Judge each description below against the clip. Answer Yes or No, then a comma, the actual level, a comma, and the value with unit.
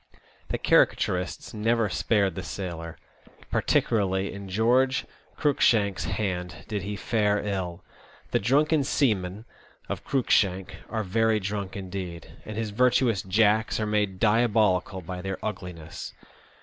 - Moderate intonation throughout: Yes, average, 3.2 semitones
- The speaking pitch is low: Yes, low, 100 Hz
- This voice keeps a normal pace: No, slow, 125 wpm